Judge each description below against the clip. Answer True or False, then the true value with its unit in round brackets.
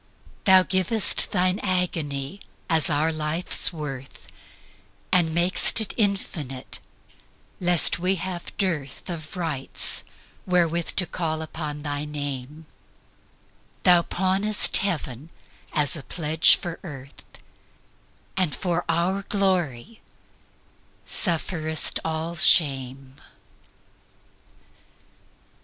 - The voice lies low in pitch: False (165 Hz)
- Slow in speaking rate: True (80 wpm)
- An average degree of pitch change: True (3.8 semitones)